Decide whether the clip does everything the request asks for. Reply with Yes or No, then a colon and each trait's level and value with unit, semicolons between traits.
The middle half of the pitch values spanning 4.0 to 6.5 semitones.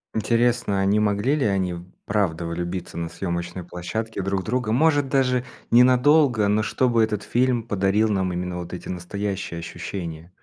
Yes: average, 5.0 semitones